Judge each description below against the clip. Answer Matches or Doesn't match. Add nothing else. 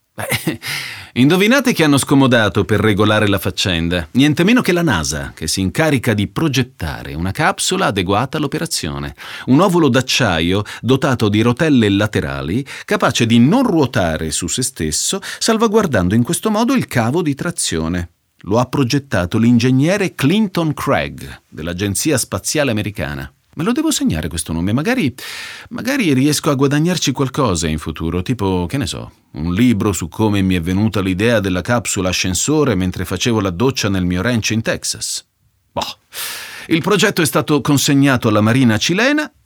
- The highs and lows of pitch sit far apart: Matches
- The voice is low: Matches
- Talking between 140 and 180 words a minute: Matches